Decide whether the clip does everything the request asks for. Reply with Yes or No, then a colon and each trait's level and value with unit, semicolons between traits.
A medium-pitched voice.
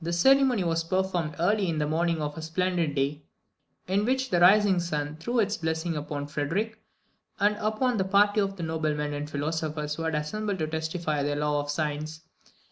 Yes: medium, 165 Hz